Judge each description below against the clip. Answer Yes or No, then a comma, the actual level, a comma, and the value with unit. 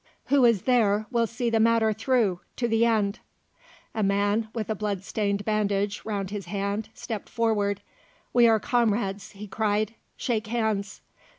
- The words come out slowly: No, average, 155 wpm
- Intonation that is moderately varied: No, narrow, 2.2 semitones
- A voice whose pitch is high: Yes, high, 215 Hz